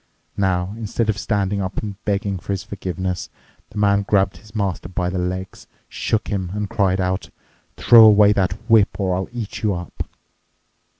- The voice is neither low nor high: No, low, 100 Hz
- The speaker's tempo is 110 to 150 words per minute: No, average, 170 wpm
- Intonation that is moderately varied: No, narrow, 2.0 semitones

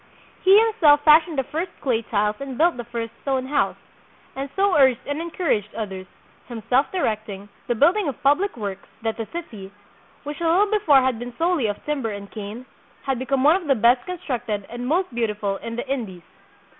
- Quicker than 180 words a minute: Yes, average, 200 wpm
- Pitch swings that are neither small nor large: No, wide, 6.2 semitones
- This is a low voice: No, very high, 260 Hz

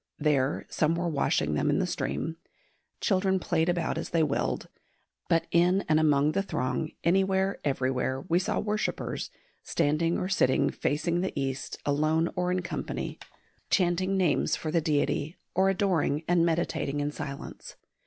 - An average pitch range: Yes, average, 3.8 semitones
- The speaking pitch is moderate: Yes, medium, 165 Hz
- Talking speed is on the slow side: No, average, 155 wpm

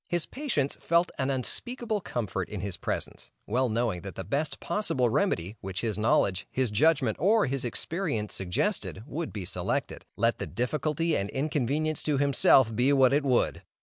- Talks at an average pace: Yes, average, 170 wpm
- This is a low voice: Yes, low, 130 Hz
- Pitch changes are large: Yes, wide, 6.3 semitones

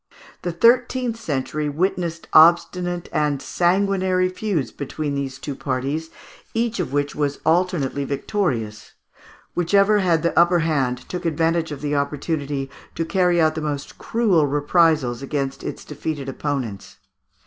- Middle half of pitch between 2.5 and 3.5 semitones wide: No, average, 4.1 semitones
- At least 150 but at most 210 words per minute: No, slow, 135 wpm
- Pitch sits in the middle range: Yes, medium, 160 Hz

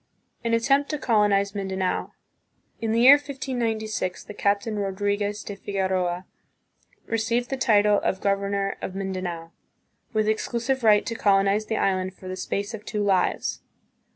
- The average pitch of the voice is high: Yes, high, 205 Hz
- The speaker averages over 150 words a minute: No, average, 145 wpm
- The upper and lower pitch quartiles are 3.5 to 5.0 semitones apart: No, average, 2.7 semitones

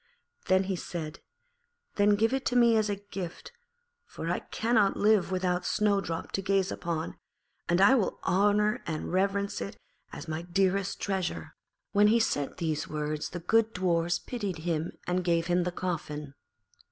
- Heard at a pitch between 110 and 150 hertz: No, medium, 185 Hz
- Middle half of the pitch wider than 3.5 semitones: No, average, 3.2 semitones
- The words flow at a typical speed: Yes, average, 165 wpm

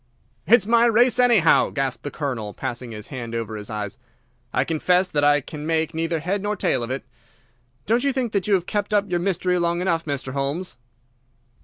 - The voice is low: No, medium, 165 Hz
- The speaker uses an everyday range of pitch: No, wide, 6.7 semitones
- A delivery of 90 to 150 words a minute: No, average, 200 wpm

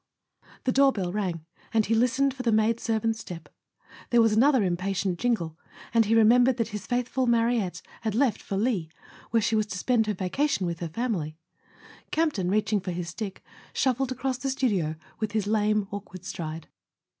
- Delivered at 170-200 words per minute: Yes, average, 180 wpm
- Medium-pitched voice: No, high, 215 Hz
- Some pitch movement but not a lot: Yes, average, 4.5 semitones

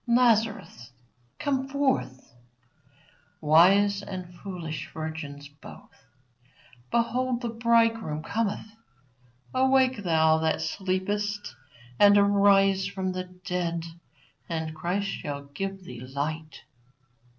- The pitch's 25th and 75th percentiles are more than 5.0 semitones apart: Yes, wide, 5.6 semitones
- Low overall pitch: No, high, 195 Hz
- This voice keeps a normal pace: No, slow, 95 wpm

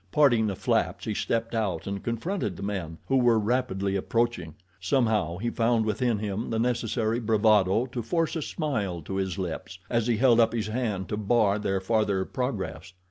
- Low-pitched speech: Yes, low, 110 Hz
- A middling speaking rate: Yes, average, 185 wpm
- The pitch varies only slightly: No, average, 3.5 semitones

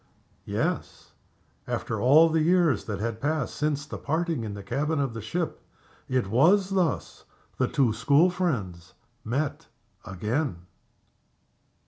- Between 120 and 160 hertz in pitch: Yes, medium, 140 Hz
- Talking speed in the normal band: No, slow, 130 wpm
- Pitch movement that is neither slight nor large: No, wide, 6.2 semitones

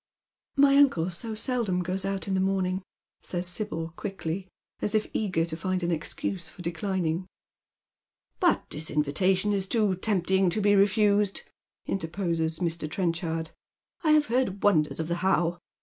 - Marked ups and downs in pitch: No, average, 3.3 semitones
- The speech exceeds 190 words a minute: No, average, 160 wpm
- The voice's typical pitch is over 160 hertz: Yes, medium, 185 Hz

